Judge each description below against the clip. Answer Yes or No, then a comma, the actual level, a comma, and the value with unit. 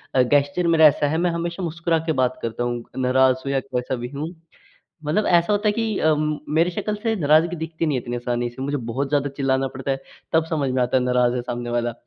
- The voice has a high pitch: No, medium, 140 Hz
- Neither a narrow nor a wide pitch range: Yes, average, 4.7 semitones